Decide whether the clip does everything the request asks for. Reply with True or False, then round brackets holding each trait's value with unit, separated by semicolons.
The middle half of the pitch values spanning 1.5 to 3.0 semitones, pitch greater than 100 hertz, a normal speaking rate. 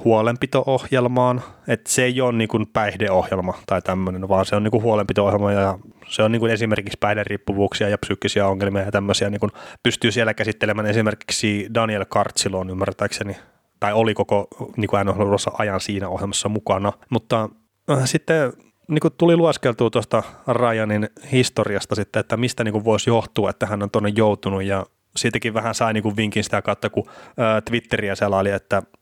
False (2.6 semitones; 110 Hz; 170 wpm)